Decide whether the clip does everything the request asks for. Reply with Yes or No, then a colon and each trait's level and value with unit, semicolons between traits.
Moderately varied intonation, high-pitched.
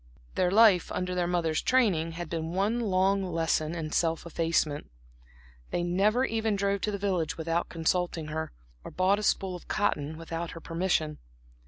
No: average, 3.2 semitones; medium, 175 Hz